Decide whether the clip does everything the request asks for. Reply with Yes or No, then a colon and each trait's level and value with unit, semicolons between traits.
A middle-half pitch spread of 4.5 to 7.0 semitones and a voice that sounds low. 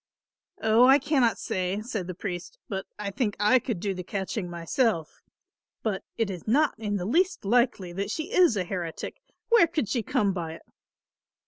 No: average, 5.2 semitones; high, 210 Hz